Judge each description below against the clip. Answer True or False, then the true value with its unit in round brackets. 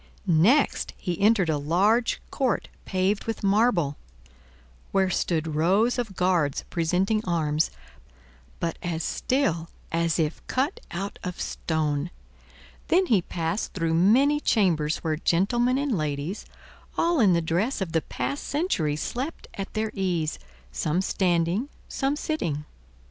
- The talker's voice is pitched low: False (185 Hz)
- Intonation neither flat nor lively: False (5.7 semitones)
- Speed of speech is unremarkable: False (130 wpm)